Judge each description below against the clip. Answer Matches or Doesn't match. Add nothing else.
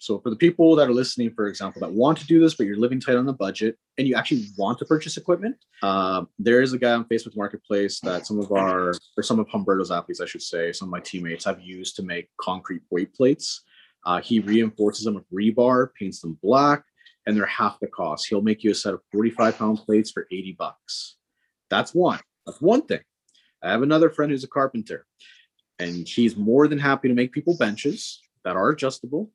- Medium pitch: Doesn't match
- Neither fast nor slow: Doesn't match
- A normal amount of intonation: Doesn't match